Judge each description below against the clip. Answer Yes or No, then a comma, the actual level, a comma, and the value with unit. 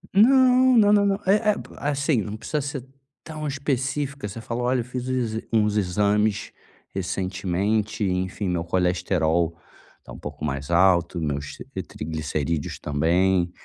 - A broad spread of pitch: Yes, wide, 7.8 semitones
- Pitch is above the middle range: No, low, 105 Hz